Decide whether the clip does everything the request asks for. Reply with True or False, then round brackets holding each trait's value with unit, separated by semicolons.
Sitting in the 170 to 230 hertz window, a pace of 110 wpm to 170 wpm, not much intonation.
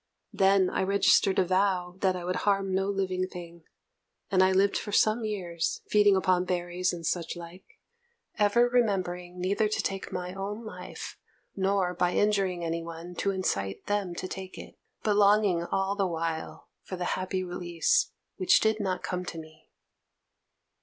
True (185 Hz; 165 wpm; 2.1 semitones)